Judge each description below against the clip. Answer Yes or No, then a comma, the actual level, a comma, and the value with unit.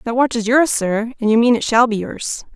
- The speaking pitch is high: Yes, high, 235 Hz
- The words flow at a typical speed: No, fast, 280 wpm